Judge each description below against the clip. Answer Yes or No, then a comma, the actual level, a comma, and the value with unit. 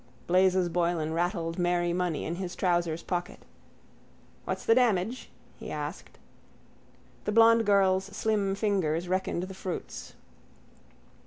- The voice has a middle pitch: Yes, medium, 180 Hz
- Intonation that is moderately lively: No, narrow, 2.3 semitones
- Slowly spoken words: Yes, slow, 115 wpm